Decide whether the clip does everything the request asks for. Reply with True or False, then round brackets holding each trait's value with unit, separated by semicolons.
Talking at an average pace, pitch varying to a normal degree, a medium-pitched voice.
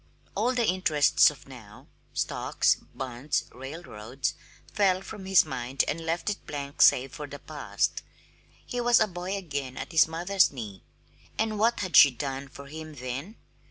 False (160 wpm; 6.0 semitones; 150 Hz)